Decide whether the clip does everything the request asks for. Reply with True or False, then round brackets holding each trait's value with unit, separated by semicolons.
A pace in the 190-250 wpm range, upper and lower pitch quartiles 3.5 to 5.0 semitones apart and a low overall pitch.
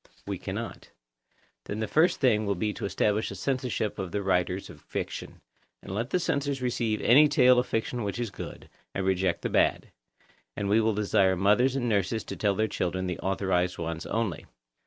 True (195 wpm; 4.3 semitones; 105 Hz)